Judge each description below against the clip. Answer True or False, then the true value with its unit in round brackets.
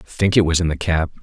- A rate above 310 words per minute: True (340 wpm)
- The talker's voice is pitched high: False (85 Hz)